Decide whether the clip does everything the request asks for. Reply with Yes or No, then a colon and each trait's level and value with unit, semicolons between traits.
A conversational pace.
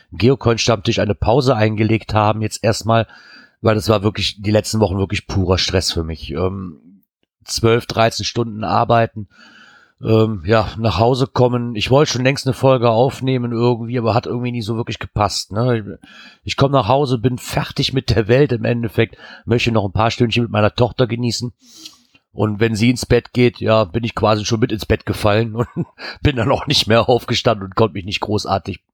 No: fast, 195 wpm